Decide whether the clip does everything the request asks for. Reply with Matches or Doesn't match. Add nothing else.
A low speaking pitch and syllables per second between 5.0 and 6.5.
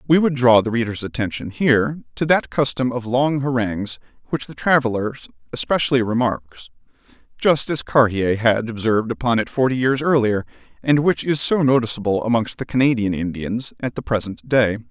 Matches